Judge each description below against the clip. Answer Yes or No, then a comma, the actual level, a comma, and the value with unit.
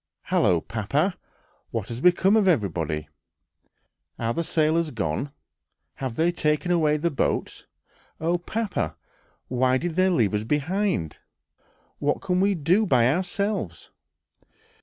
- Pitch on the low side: No, medium, 155 Hz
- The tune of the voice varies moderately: No, wide, 7.5 semitones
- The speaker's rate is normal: No, slow, 125 wpm